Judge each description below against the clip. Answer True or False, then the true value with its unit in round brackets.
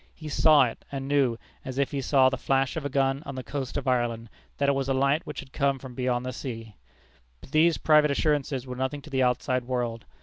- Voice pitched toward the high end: False (135 Hz)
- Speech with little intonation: True (2.0 semitones)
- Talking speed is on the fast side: True (240 wpm)